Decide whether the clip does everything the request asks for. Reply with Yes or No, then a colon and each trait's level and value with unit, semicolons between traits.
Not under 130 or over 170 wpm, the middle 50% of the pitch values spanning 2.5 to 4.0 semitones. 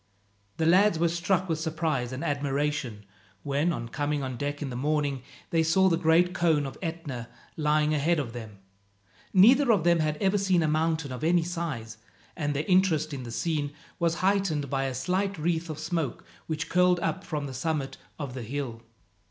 No: average, 190 wpm; average, 3.5 semitones